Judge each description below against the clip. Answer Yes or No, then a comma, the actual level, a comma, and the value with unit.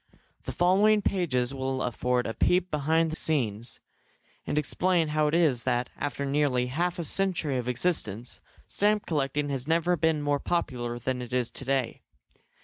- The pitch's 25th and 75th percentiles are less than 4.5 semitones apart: No, average, 5.0 semitones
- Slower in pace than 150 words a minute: No, average, 165 wpm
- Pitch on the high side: No, medium, 145 Hz